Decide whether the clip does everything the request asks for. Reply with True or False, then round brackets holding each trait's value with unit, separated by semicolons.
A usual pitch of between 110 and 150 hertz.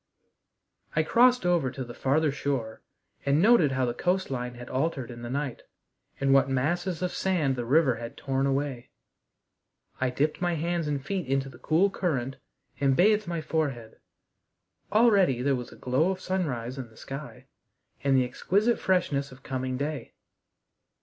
True (140 Hz)